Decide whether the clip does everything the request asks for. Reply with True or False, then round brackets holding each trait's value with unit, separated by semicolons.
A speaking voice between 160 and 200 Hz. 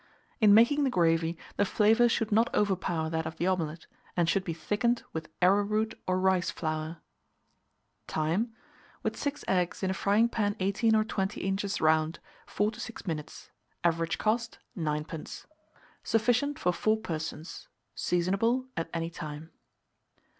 True (190 Hz)